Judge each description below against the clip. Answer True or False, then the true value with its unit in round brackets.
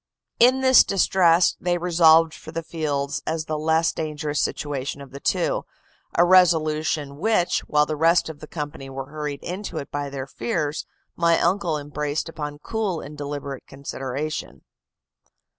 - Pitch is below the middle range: False (155 Hz)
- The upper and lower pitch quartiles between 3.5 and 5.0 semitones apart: False (2.7 semitones)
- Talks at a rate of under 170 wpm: True (155 wpm)